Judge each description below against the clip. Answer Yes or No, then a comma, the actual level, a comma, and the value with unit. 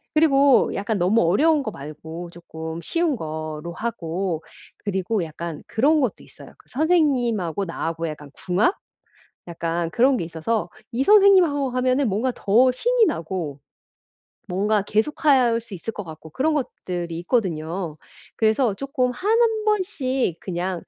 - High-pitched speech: Yes, high, 215 Hz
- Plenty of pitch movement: Yes, wide, 8.1 semitones